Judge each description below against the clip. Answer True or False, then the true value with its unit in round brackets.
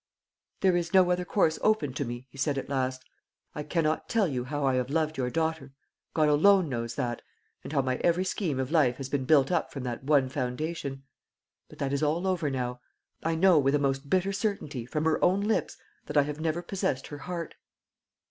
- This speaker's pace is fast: True (215 wpm)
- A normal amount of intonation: True (4.2 semitones)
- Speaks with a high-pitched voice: False (150 Hz)